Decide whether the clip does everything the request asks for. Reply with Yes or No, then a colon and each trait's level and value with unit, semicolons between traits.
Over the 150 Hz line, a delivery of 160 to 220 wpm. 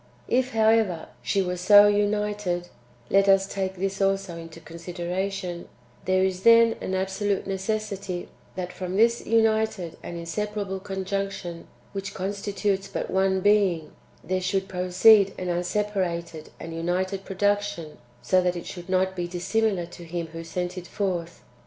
No: high, 190 Hz; average, 150 wpm